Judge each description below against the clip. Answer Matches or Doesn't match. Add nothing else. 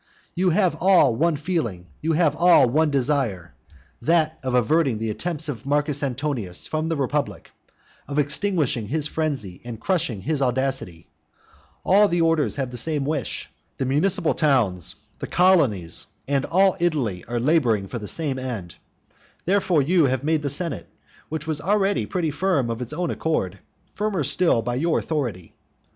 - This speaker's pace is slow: Doesn't match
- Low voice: Doesn't match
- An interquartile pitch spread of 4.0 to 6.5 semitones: Matches